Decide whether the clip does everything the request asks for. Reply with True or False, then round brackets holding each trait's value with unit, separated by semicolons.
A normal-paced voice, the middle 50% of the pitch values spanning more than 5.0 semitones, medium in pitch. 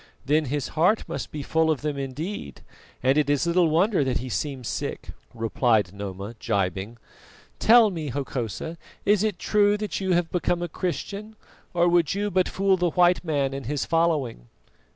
True (175 wpm; 5.6 semitones; 155 Hz)